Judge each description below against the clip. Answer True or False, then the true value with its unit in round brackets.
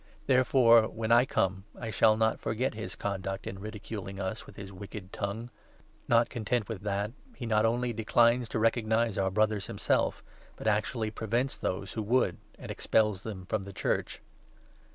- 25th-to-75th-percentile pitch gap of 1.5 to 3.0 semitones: True (2.7 semitones)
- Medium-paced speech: True (175 wpm)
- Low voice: True (110 Hz)